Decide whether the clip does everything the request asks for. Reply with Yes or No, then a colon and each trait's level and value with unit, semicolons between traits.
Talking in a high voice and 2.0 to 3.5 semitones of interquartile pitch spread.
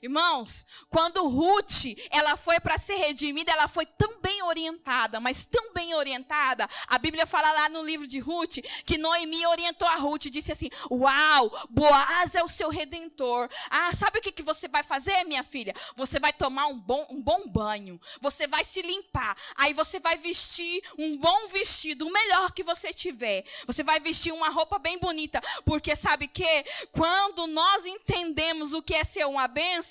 Yes: very high, 320 Hz; average, 2.8 semitones